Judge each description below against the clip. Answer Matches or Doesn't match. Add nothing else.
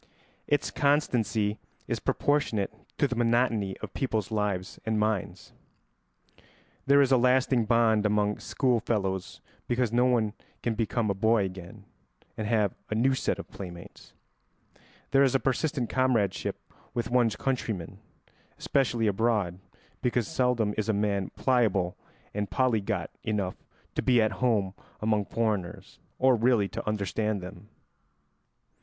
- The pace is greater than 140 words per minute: Doesn't match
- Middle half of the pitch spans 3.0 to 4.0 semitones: Matches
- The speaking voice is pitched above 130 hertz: Doesn't match